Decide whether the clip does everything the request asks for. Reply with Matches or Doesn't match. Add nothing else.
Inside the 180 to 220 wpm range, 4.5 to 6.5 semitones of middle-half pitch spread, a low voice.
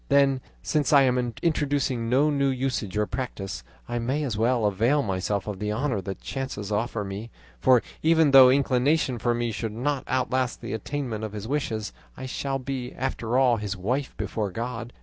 Doesn't match